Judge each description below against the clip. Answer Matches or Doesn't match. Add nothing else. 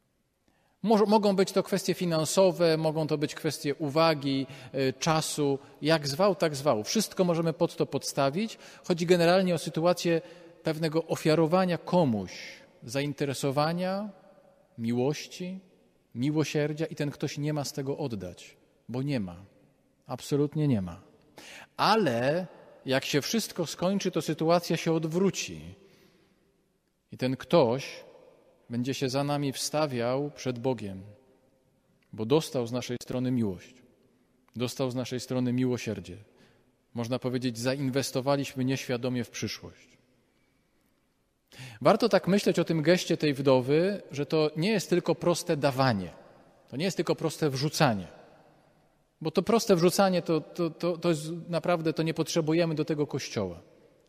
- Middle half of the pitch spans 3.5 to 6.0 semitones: Matches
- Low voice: Doesn't match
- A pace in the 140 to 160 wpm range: Doesn't match